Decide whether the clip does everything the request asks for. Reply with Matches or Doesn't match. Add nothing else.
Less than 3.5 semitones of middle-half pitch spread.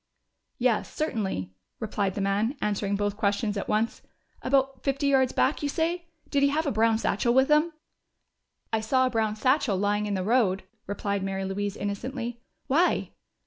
Doesn't match